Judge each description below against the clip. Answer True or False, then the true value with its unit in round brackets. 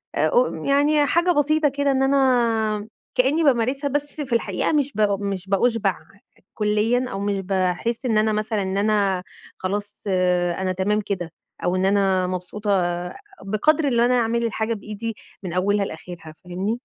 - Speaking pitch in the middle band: False (215 Hz)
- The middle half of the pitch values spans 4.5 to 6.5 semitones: True (5.1 semitones)